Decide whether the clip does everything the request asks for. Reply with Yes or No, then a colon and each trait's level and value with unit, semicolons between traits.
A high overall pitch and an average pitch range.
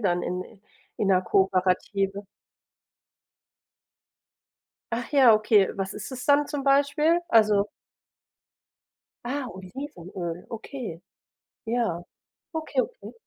No: high, 215 Hz; wide, 6.3 semitones